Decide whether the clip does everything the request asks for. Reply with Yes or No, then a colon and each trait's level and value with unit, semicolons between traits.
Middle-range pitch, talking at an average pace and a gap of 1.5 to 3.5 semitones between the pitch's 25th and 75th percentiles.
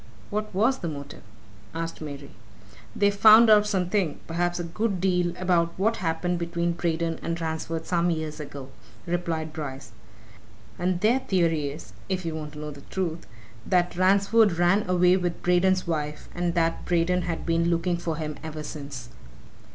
Yes: medium, 170 Hz; average, 165 wpm; narrow, 2.5 semitones